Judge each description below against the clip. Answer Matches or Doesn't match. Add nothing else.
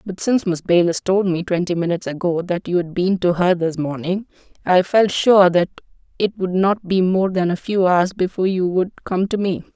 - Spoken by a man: Doesn't match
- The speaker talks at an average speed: Doesn't match